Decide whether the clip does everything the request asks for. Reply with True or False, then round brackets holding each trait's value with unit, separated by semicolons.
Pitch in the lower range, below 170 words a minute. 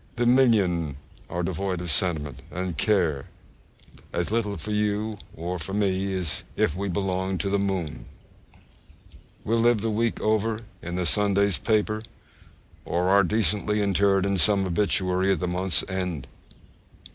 True (95 Hz; 145 wpm)